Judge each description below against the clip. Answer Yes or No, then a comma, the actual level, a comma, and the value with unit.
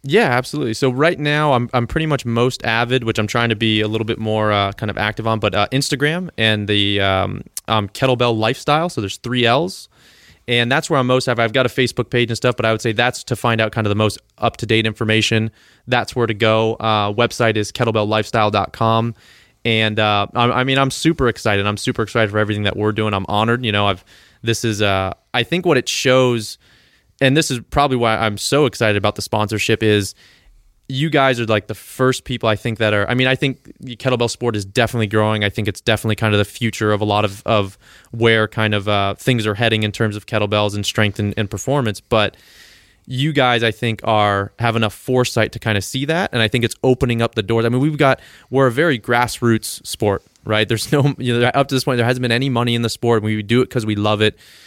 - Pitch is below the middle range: Yes, low, 115 Hz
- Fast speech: Yes, fast, 240 wpm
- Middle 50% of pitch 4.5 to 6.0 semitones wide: No, average, 2.9 semitones